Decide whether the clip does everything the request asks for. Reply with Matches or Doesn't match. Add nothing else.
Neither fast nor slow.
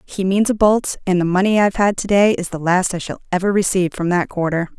Doesn't match